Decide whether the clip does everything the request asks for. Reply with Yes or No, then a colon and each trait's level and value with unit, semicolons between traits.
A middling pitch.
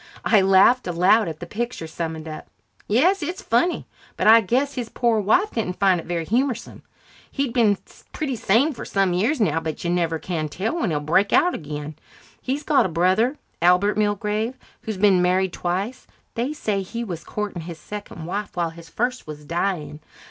No: high, 200 Hz